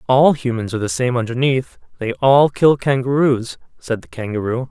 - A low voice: Yes, low, 125 Hz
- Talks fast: No, average, 165 wpm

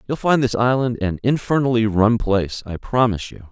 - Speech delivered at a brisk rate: No, average, 190 wpm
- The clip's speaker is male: Yes, male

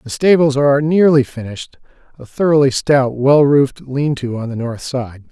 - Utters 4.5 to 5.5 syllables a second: Yes, 5.0 syllables/s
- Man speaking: Yes, male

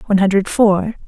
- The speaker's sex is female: Yes, female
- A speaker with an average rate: Yes, average, 165 wpm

